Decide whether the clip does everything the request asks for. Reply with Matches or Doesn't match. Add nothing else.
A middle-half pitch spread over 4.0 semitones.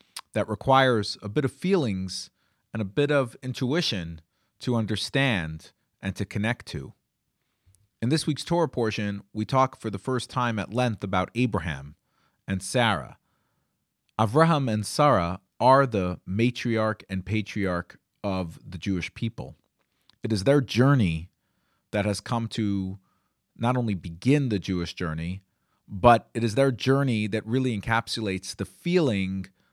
Matches